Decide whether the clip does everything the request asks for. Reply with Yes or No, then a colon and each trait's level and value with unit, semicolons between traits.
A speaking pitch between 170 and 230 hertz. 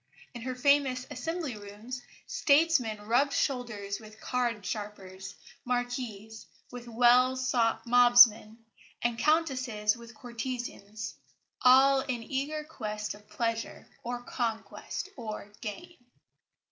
No: high, 240 Hz